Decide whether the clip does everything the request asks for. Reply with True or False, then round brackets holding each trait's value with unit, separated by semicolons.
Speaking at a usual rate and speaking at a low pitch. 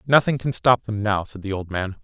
False (265 wpm; 110 Hz)